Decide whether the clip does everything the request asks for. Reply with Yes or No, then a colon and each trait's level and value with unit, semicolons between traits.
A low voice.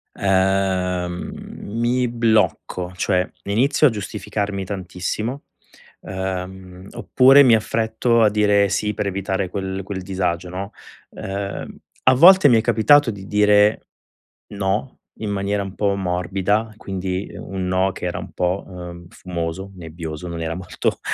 Yes: very low, 95 Hz